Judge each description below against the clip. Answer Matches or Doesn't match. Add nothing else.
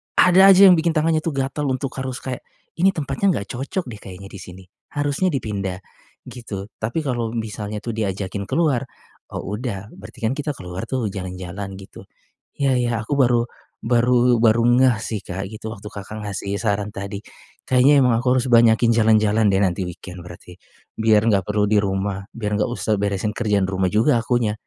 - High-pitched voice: Doesn't match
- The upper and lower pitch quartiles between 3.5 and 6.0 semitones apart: Matches